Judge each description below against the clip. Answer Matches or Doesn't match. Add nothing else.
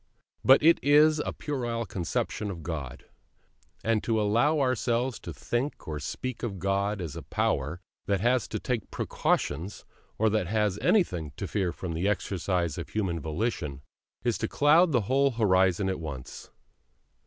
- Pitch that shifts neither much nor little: Doesn't match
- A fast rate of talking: Doesn't match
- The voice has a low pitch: Matches